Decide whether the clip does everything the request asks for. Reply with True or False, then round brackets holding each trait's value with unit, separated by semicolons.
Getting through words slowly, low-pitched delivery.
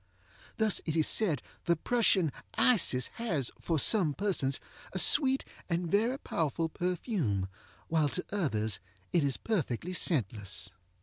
False (130 wpm; 170 Hz)